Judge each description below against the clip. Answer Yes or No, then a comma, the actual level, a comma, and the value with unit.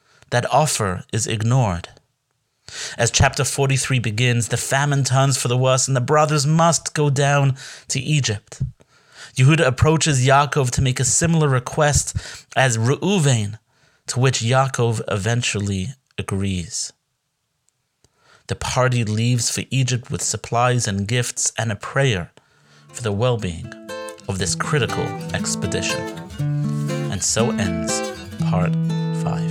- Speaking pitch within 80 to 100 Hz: No, low, 125 Hz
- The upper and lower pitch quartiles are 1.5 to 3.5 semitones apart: No, average, 4.0 semitones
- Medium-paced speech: No, slow, 125 wpm